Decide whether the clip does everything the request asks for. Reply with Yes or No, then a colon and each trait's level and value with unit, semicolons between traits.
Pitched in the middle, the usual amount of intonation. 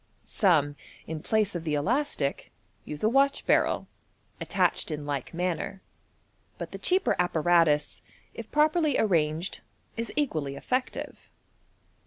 No: medium, 175 Hz; wide, 8.8 semitones